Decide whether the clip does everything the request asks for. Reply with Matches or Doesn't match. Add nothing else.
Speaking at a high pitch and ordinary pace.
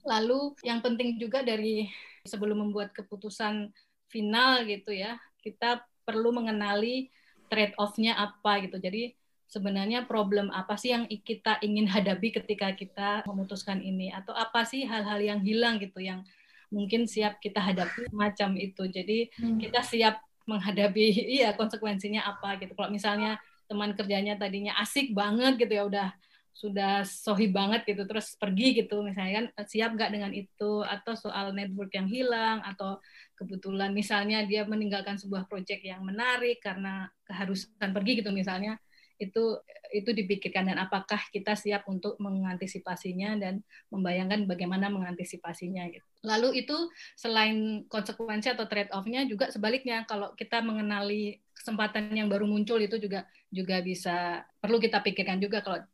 Doesn't match